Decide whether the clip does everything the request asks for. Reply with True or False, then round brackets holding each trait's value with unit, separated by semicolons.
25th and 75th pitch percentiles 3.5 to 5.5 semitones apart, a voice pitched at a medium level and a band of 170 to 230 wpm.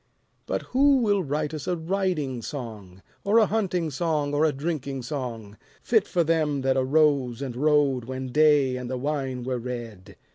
True (4.1 semitones; 145 Hz; 175 wpm)